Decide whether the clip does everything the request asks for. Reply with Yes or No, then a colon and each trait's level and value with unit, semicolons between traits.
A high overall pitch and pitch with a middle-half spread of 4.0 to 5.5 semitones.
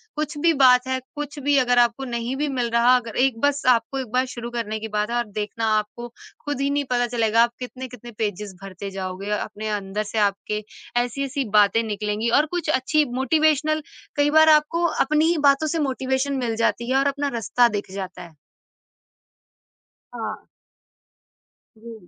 Yes: high, 245 Hz; average, 4.5 semitones